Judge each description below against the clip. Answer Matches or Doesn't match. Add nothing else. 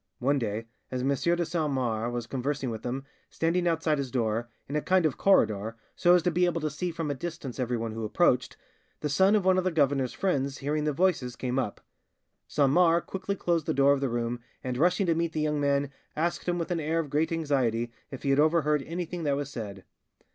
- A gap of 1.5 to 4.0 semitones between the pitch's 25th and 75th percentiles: Doesn't match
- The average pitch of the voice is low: Doesn't match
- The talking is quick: Matches